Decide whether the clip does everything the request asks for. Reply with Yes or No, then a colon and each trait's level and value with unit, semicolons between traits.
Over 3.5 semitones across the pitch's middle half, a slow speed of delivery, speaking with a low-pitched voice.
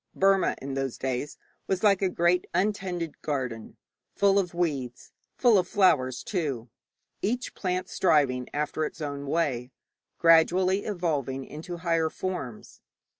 No: wide, 5.5 semitones; slow, 130 wpm; medium, 165 Hz